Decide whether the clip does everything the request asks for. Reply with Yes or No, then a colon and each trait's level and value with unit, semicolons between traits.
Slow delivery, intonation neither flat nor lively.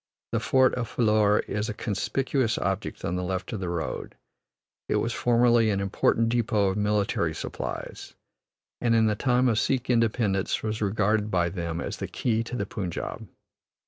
No: average, 175 wpm; average, 3.1 semitones